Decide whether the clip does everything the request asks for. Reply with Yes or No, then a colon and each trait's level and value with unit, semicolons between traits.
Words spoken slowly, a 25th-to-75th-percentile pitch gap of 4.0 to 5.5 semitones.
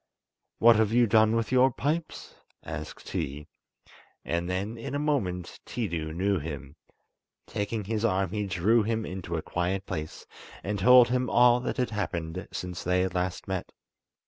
No: average, 165 wpm; average, 4.5 semitones